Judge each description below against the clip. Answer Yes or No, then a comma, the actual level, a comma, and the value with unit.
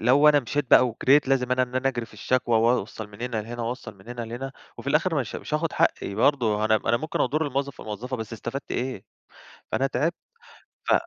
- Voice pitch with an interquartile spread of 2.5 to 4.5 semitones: Yes, average, 3.3 semitones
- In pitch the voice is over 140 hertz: No, low, 125 Hz